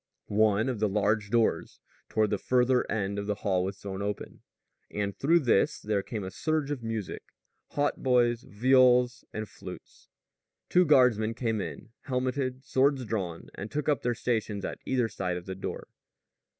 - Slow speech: No, average, 165 wpm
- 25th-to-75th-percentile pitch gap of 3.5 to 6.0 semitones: Yes, average, 4.0 semitones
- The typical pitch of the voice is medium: No, low, 110 Hz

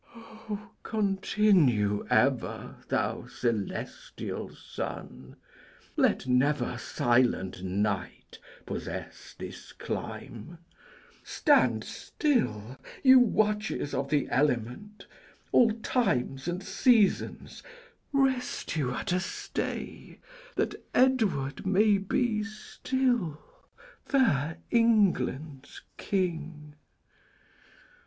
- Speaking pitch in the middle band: Yes, medium, 170 Hz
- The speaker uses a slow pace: Yes, slow, 75 wpm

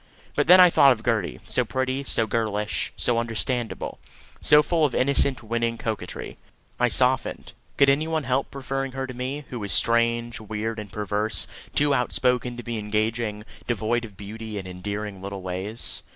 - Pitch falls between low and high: No, low, 115 Hz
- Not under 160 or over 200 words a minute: Yes, average, 170 wpm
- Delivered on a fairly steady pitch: No, average, 3.6 semitones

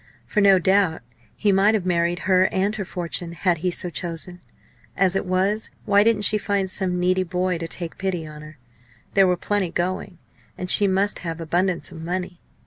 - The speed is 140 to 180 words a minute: No, average, 195 wpm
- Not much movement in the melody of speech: Yes, narrow, 2.1 semitones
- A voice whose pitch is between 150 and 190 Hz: Yes, medium, 185 Hz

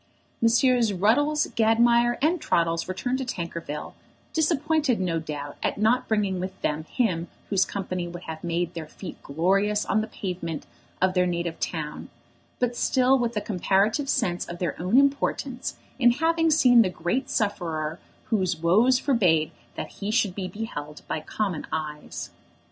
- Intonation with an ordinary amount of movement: No, wide, 6.1 semitones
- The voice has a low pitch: No, high, 195 Hz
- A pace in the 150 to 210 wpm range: Yes, average, 155 wpm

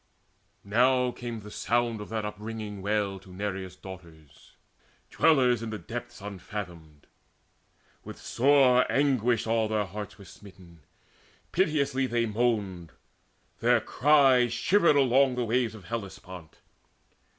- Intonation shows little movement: No, average, 4.1 semitones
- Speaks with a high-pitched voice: No, low, 110 Hz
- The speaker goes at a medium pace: No, slow, 120 wpm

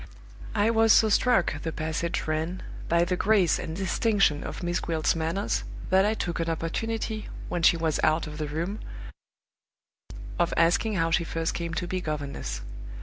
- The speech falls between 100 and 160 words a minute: No, average, 170 wpm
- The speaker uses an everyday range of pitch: Yes, average, 3.5 semitones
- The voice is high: No, medium, 170 Hz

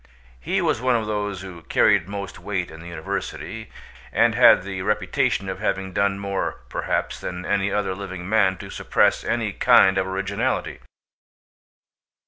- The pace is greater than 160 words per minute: No, average, 155 wpm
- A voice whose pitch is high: No, low, 100 Hz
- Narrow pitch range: Yes, narrow, 1.7 semitones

